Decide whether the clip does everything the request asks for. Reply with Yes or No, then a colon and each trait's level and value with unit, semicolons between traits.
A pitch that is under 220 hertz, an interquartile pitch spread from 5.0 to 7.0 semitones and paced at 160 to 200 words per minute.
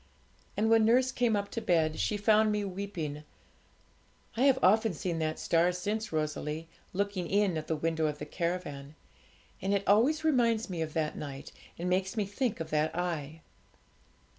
Yes: medium, 185 Hz; average, 5.3 semitones; average, 175 wpm